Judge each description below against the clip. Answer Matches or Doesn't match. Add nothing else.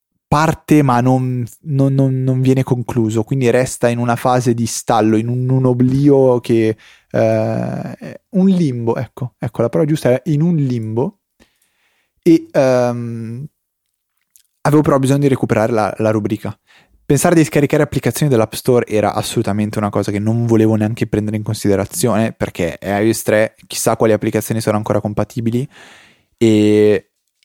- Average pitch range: Matches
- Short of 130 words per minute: Doesn't match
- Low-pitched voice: Matches